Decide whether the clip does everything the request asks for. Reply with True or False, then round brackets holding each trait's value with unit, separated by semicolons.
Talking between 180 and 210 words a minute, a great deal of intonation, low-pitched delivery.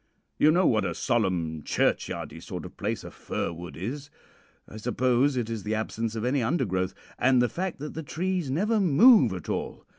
True (190 wpm; 6.1 semitones; 125 Hz)